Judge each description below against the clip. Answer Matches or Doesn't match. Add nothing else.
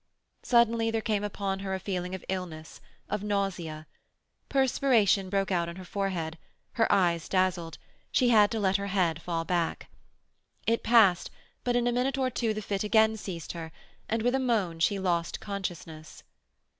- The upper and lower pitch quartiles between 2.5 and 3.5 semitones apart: Doesn't match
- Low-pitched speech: Doesn't match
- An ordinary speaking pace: Matches